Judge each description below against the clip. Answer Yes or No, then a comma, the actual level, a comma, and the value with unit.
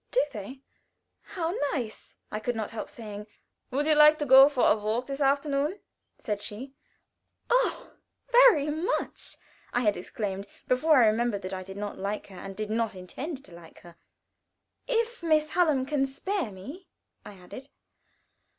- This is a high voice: Yes, very high, 255 Hz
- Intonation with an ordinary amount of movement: No, wide, 6.5 semitones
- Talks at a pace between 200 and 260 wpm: No, average, 165 wpm